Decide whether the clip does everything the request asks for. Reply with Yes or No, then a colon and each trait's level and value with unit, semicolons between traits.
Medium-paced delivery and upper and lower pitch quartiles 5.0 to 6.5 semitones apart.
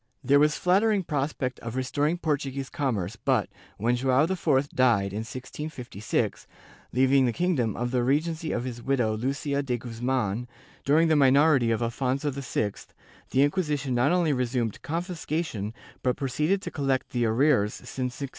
No: average, 155 wpm; average, 3.7 semitones